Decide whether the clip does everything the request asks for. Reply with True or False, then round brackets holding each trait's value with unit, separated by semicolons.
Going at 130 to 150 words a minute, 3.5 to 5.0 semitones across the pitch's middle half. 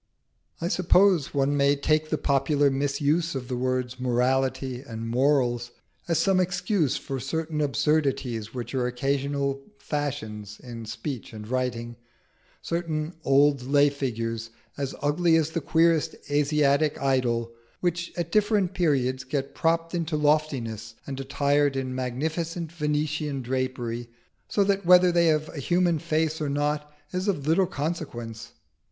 True (140 wpm; 4.0 semitones)